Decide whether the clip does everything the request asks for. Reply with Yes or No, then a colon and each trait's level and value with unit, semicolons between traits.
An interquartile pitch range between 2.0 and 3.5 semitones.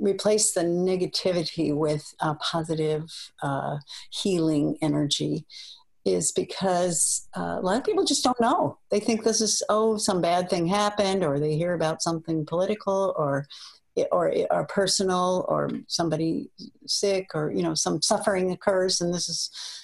No: average, 4.3 semitones